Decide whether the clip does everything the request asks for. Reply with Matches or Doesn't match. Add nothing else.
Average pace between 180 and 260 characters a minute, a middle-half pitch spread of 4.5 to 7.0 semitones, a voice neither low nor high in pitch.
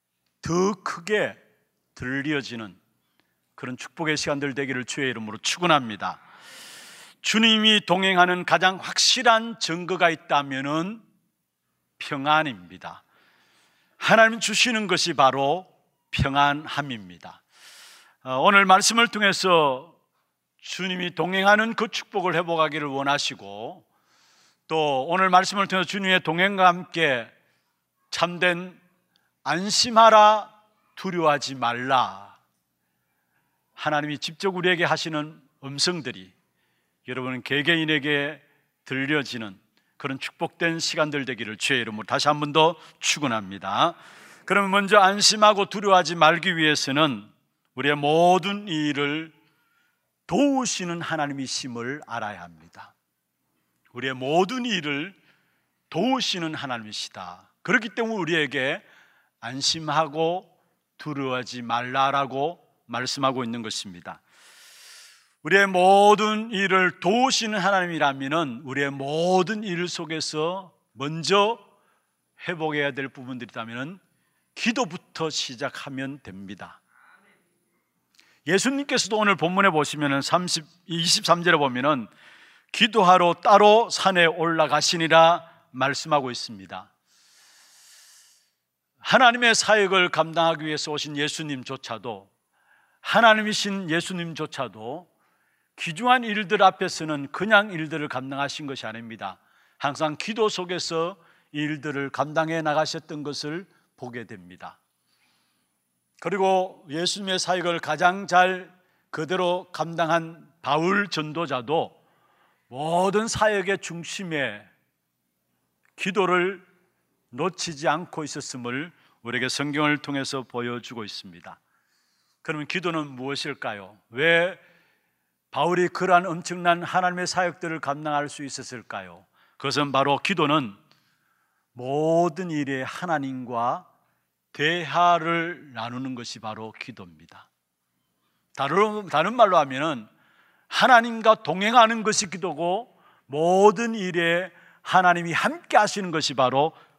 Matches